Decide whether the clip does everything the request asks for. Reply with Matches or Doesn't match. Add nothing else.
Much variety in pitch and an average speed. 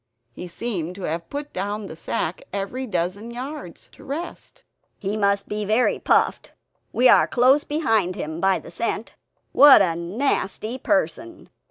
Matches